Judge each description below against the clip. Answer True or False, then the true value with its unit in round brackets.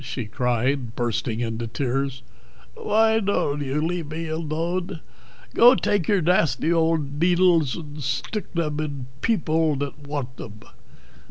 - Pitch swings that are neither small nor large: True (4.6 semitones)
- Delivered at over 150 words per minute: False (135 wpm)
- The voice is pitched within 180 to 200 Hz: False (150 Hz)